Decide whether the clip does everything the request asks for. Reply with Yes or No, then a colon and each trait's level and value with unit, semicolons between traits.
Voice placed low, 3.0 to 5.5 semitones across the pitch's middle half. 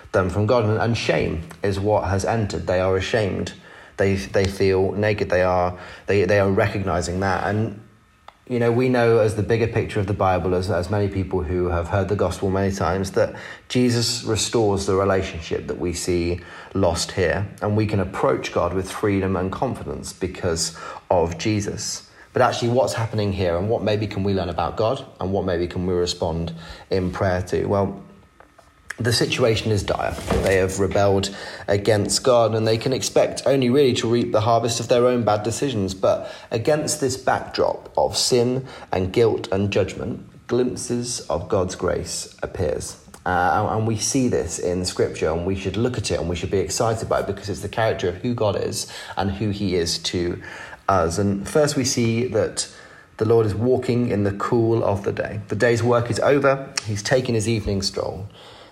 Yes: low, 100 Hz; average, 3.5 semitones